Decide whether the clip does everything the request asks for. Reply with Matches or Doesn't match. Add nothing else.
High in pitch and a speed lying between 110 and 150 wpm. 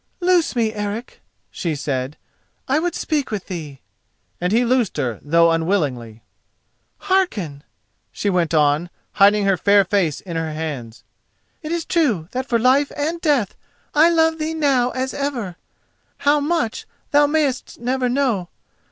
Matches